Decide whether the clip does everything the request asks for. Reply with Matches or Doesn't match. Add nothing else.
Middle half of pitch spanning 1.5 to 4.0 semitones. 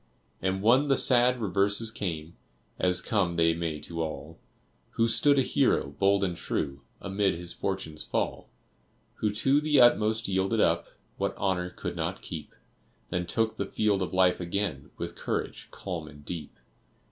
Doesn't match